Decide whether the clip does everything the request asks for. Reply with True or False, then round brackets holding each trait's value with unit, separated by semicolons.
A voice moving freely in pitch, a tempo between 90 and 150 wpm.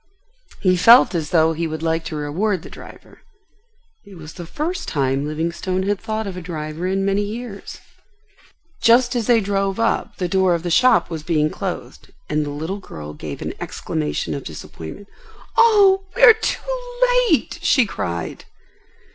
False (6.4 semitones; 170 wpm)